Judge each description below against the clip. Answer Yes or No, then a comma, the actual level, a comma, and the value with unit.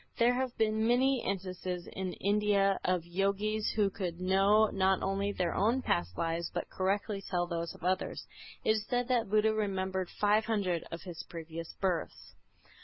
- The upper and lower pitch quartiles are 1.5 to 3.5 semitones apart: Yes, average, 3.0 semitones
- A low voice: No, high, 195 Hz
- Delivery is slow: No, average, 170 wpm